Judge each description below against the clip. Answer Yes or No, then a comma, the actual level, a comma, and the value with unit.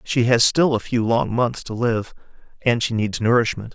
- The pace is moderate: No, fast, 210 wpm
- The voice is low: Yes, low, 120 Hz